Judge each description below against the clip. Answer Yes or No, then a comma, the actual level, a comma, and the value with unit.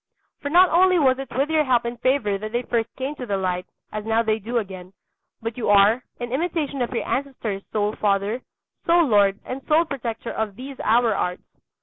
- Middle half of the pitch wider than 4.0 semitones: Yes, average, 4.6 semitones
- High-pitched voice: Yes, high, 235 Hz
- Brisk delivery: Yes, fast, 210 wpm